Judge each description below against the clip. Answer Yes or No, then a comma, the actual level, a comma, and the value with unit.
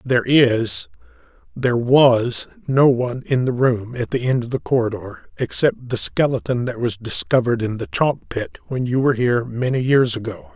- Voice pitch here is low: Yes, low, 125 Hz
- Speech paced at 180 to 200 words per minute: No, average, 170 wpm